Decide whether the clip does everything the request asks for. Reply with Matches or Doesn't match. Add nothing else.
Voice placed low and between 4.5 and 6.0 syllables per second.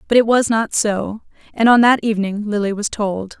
Doesn't match